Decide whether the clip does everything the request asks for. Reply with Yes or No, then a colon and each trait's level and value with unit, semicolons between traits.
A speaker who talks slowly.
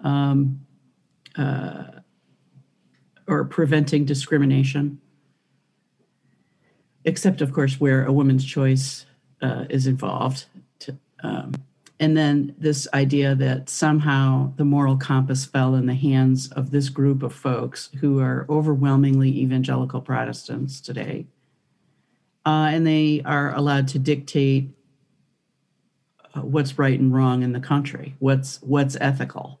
Yes: slow, 120 wpm